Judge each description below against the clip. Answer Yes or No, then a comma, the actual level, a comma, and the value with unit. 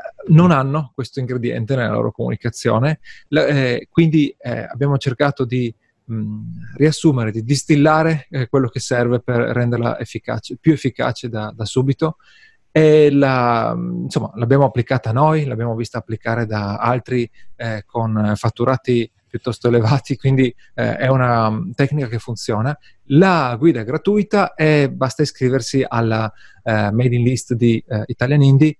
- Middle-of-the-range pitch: No, low, 125 Hz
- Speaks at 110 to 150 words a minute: Yes, average, 145 wpm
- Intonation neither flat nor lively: Yes, average, 3.7 semitones